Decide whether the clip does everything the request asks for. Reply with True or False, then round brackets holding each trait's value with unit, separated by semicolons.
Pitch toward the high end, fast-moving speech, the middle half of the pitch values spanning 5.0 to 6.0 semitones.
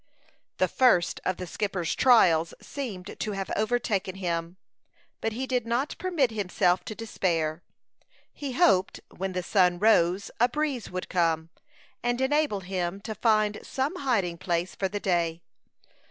False (195 Hz; 150 wpm; 5.4 semitones)